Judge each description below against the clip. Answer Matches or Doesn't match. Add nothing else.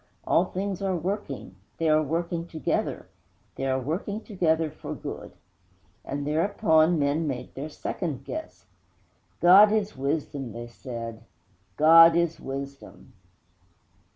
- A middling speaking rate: Doesn't match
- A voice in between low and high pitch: Matches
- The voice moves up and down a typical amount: Matches